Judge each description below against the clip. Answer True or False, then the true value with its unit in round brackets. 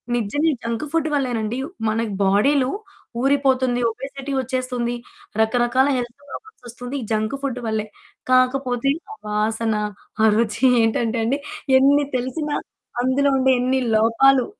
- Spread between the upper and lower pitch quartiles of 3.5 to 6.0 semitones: False (2.9 semitones)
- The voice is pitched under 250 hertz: False (255 Hz)